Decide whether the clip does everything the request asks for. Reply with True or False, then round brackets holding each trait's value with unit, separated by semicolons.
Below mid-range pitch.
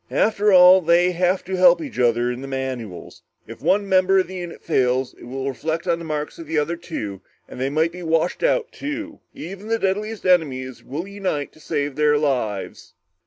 False (165 Hz)